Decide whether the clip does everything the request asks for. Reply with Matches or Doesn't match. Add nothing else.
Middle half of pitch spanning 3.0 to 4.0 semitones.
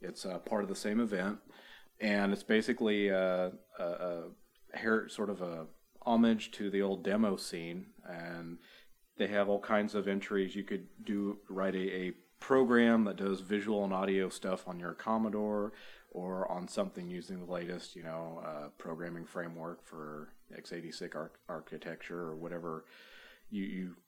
Matches